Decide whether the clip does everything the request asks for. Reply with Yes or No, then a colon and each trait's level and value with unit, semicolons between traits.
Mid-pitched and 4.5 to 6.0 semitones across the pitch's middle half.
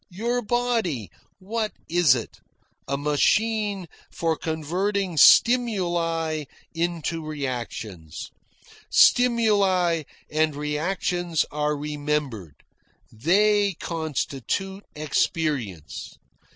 Yes: medium, 165 Hz; average, 5.1 semitones